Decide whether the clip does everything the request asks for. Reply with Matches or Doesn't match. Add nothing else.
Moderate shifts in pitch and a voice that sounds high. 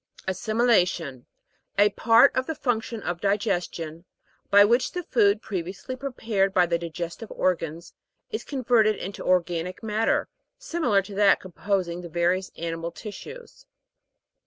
Matches